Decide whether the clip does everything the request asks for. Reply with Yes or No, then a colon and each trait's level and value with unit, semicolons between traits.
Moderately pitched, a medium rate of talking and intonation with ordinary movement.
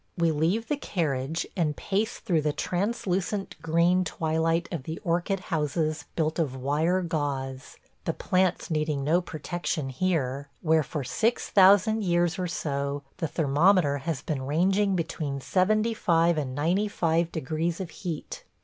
Yes: medium, 165 Hz; average, 150 wpm; average, 3.7 semitones